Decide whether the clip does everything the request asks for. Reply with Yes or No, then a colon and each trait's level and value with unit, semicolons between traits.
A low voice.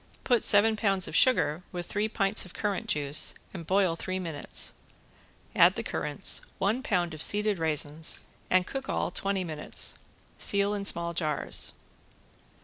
No: medium, 185 Hz